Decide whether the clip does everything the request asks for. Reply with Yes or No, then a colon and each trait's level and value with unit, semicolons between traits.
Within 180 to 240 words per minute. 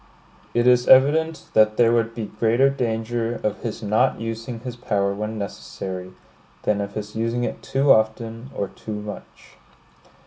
No: average, 160 wpm